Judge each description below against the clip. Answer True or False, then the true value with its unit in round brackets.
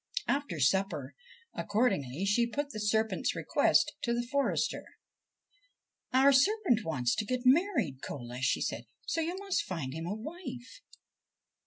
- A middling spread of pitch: False (8.9 semitones)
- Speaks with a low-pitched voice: False (235 Hz)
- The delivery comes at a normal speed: True (150 wpm)